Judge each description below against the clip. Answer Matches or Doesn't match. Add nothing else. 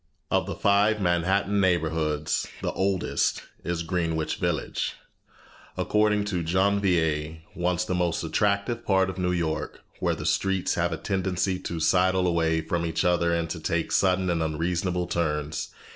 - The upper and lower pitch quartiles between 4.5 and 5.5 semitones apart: Doesn't match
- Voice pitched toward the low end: Matches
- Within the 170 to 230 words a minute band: Doesn't match